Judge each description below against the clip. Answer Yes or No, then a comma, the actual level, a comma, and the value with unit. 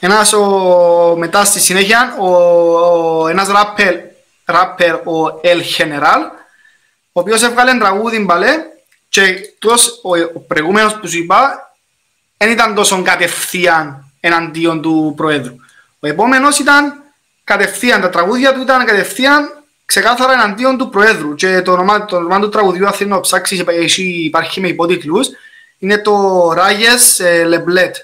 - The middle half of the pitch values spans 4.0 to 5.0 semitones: Yes, average, 4.6 semitones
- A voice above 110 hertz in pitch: Yes, high, 190 Hz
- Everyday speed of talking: Yes, average, 135 wpm